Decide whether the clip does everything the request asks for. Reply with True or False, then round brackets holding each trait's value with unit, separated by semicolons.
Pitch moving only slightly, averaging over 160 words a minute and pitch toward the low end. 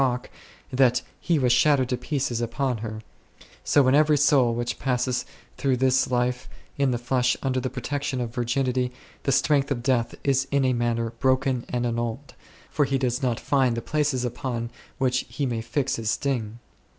True (2.2 semitones; 180 wpm; 125 Hz)